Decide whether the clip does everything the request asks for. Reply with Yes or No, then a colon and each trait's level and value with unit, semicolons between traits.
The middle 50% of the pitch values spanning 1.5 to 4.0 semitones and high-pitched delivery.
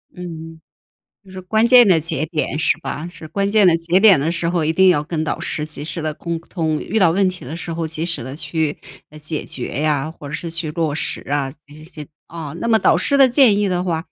No: average, 3.0 semitones; medium, 165 Hz